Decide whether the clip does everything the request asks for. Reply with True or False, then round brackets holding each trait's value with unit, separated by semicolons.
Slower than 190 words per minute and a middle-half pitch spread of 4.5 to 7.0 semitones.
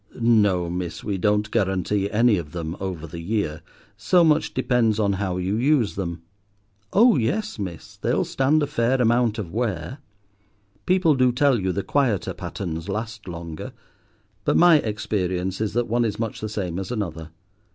True (170 wpm; 5.0 semitones)